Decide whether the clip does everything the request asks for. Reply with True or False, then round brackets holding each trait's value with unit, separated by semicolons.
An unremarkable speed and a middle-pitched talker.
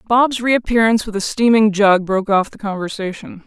False (175 wpm; 210 Hz)